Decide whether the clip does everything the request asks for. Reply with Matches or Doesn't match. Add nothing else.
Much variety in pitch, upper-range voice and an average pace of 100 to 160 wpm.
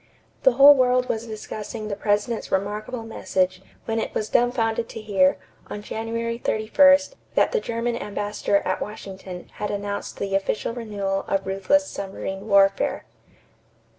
Doesn't match